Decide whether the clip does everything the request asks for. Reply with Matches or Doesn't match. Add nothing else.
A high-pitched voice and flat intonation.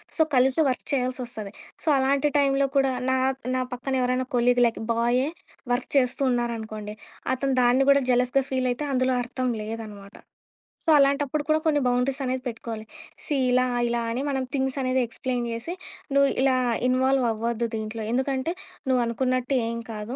Matches